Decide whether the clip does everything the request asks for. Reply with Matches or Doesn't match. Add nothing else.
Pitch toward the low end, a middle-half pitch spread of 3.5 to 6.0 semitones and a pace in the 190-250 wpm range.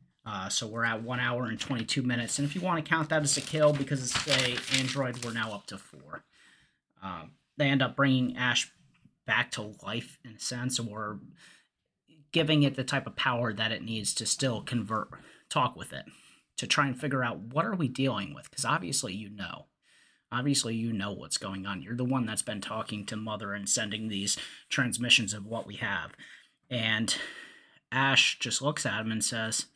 Matches